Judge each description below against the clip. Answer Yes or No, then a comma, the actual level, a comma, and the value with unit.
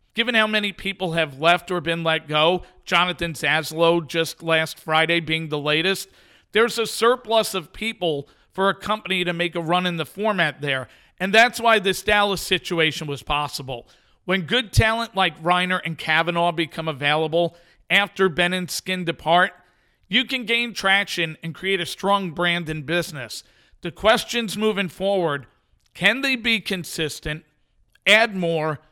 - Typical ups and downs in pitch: Yes, average, 3.7 semitones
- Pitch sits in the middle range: Yes, medium, 175 Hz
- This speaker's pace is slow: No, average, 160 wpm